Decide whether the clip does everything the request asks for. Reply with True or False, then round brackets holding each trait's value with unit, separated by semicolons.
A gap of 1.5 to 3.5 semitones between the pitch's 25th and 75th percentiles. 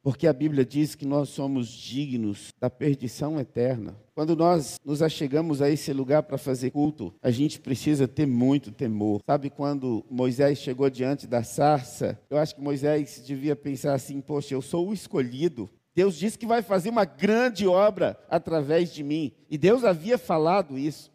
True (2.9 semitones)